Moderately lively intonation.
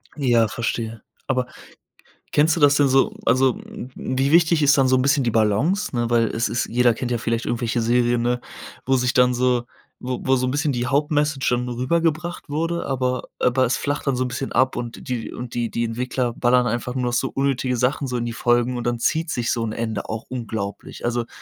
No: narrow, 2.2 semitones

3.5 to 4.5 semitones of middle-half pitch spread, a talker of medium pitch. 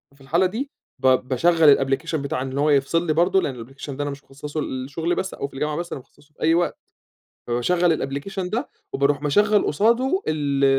Yes: average, 4.1 semitones; medium, 150 Hz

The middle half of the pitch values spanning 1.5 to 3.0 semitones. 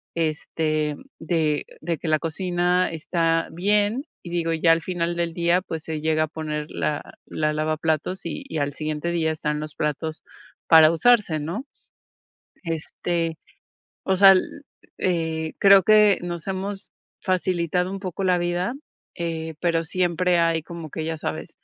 Yes: narrow, 2.4 semitones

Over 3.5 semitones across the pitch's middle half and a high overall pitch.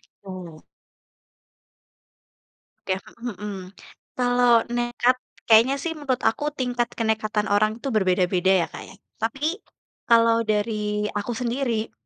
No: average, 2.9 semitones; high, 225 Hz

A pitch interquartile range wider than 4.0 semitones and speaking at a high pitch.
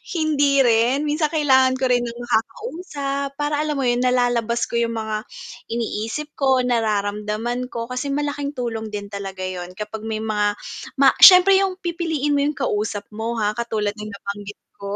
Yes: average, 4.8 semitones; high, 240 Hz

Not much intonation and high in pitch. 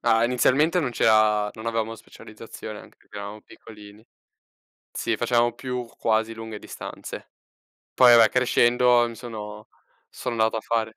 No: narrow, 1.7 semitones; low, 115 Hz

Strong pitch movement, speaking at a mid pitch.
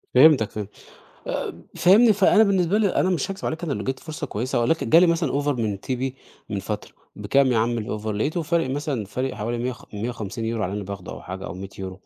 No: wide, 7.4 semitones; low, 130 Hz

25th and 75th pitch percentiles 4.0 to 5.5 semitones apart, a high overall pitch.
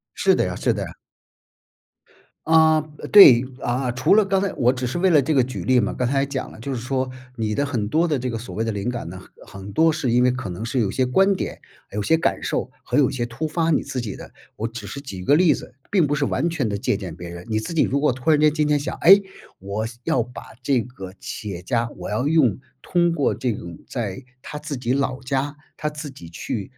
No: average, 4.8 semitones; low, 130 Hz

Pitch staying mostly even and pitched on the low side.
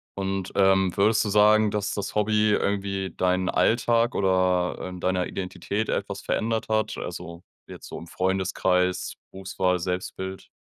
Yes: narrow, 2.3 semitones; very low, 95 Hz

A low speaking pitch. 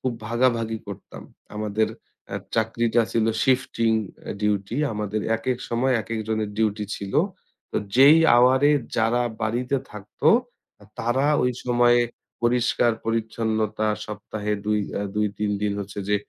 Yes: low, 110 Hz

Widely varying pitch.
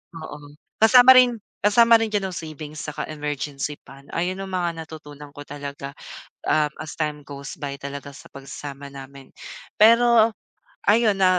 Yes: wide, 6.2 semitones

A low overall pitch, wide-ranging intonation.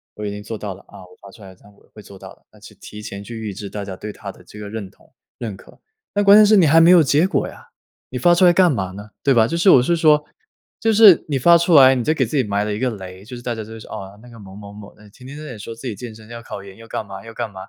Yes: low, 110 Hz; wide, 6.0 semitones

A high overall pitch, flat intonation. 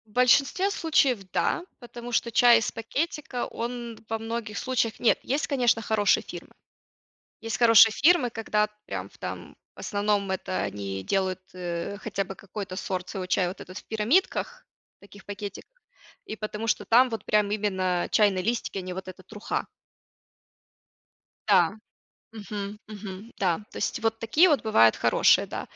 No: high, 215 Hz; average, 3.5 semitones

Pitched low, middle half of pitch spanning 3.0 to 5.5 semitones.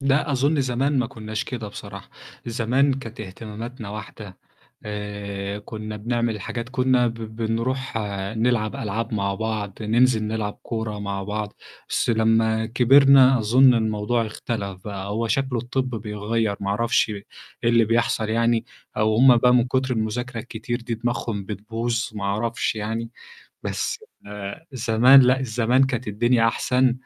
No: low, 115 Hz; narrow, 2.6 semitones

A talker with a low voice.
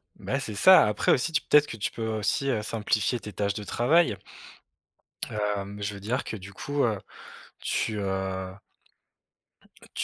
Yes: low, 105 Hz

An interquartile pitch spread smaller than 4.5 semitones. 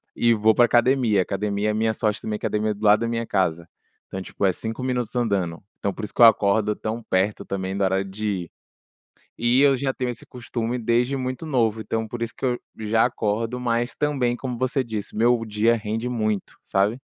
Yes: narrow, 2.6 semitones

